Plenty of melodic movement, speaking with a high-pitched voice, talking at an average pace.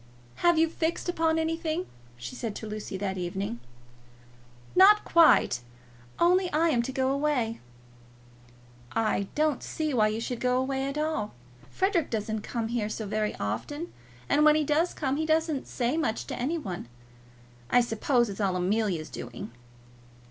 Yes: wide, 6.8 semitones; very high, 260 Hz; average, 160 wpm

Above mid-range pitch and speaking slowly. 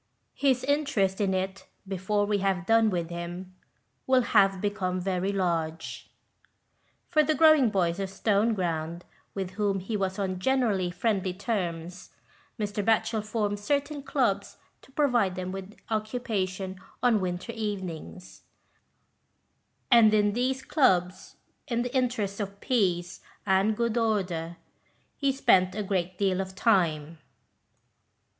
Yes: high, 200 Hz; slow, 130 wpm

